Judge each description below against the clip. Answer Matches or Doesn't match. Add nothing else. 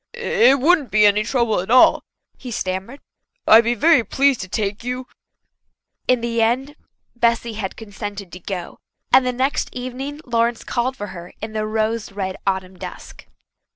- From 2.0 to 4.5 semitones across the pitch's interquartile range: Matches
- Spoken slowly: Doesn't match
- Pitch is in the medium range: Doesn't match